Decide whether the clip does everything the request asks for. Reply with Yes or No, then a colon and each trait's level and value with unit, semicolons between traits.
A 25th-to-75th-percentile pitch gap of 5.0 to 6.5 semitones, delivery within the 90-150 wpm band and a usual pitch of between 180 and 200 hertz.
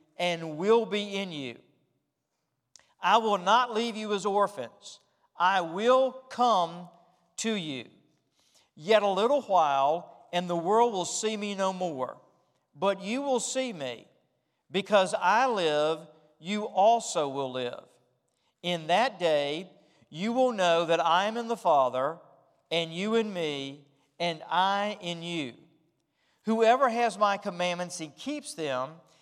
Yes: average, 5.3 semitones; average, 140 wpm; medium, 185 Hz